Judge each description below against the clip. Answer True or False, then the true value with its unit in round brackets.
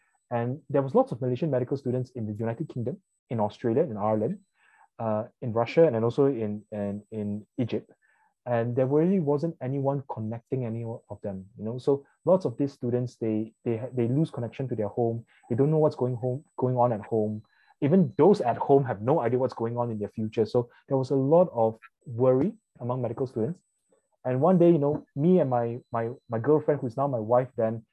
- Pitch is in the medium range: False (125 Hz)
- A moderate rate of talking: False (215 wpm)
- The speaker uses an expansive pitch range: False (3.7 semitones)